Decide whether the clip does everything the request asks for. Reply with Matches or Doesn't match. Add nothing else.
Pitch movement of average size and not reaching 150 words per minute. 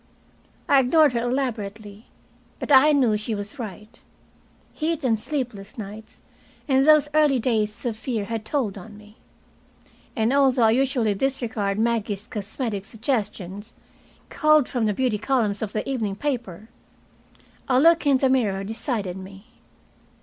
Matches